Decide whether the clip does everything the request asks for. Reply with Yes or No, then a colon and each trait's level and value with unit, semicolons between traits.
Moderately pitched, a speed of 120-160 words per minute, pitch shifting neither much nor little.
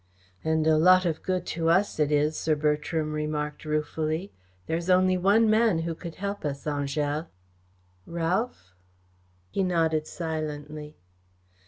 Yes: medium, 160 Hz; average, 140 wpm; average, 3.2 semitones